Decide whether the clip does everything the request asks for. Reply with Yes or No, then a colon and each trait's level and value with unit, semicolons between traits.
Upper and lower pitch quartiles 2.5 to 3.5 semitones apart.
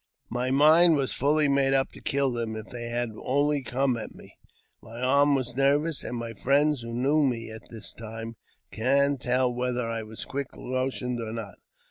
Yes: average, 3.1 semitones